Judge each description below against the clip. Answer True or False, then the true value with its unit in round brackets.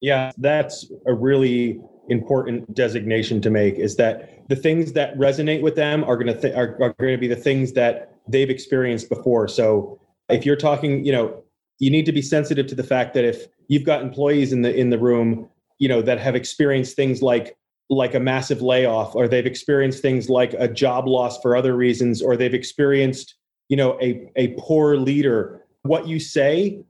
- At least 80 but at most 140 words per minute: False (200 wpm)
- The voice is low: True (130 Hz)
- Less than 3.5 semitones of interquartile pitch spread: True (2.6 semitones)